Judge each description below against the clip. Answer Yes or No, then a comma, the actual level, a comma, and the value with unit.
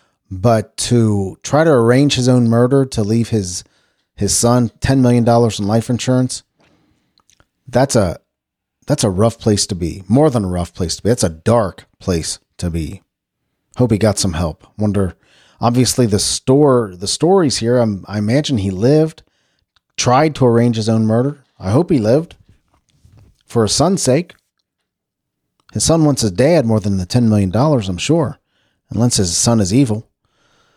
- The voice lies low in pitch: Yes, low, 115 Hz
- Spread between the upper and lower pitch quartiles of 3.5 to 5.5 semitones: Yes, average, 4.0 semitones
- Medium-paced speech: Yes, average, 175 wpm